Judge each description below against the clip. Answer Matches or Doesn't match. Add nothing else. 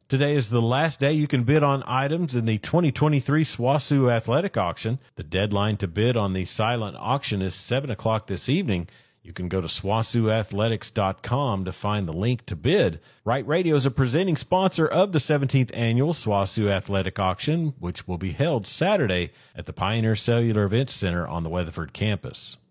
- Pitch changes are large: Matches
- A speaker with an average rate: Matches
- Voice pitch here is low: Matches